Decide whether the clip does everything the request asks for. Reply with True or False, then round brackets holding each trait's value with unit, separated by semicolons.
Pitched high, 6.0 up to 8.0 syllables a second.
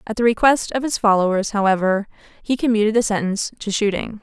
True (210 Hz; 6.3 syllables/s)